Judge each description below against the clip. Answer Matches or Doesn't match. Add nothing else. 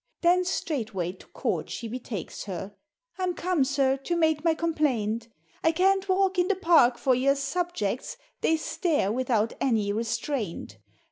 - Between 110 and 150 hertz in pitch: Doesn't match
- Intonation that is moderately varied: Doesn't match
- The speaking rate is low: Doesn't match